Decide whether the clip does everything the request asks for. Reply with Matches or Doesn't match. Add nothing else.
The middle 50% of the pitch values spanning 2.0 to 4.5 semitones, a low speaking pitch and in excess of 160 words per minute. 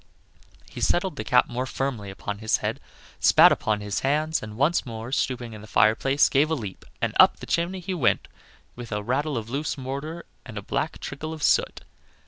Doesn't match